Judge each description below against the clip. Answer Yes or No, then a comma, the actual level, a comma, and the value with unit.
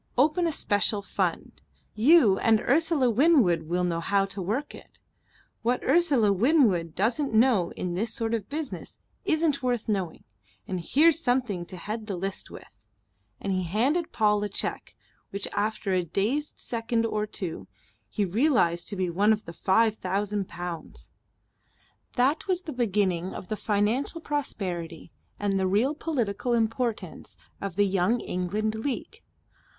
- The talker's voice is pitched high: Yes, high, 215 Hz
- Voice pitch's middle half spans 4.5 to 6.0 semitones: Yes, average, 5.1 semitones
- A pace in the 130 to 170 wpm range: Yes, average, 150 wpm